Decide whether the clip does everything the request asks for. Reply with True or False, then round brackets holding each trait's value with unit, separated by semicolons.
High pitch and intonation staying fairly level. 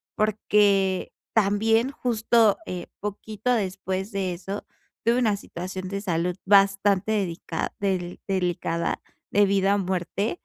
True (195 Hz; 2.1 semitones)